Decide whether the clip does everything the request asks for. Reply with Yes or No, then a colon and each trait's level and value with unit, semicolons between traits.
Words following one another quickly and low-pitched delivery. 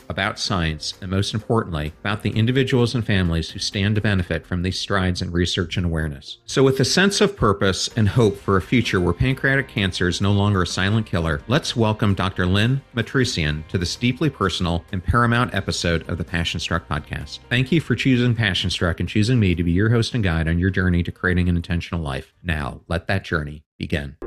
Yes: fast, 215 wpm; very low, 95 Hz